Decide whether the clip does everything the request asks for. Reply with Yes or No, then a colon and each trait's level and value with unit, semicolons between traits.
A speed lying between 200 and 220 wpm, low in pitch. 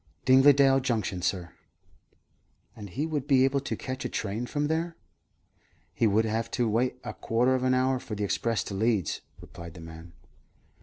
No: average, 175 wpm; low, 120 Hz